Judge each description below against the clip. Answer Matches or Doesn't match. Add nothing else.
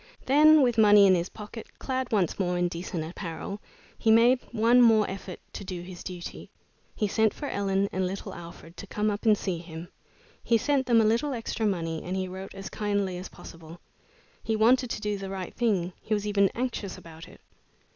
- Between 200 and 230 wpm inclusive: Matches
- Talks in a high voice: Matches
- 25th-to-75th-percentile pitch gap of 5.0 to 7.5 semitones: Doesn't match